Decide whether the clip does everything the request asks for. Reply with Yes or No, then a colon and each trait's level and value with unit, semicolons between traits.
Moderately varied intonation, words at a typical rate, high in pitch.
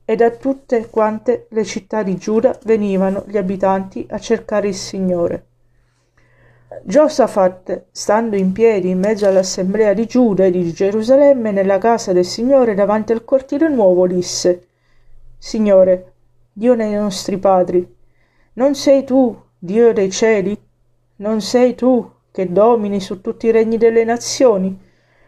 Yes: average, 3.7 semitones; average, 140 wpm; high, 205 Hz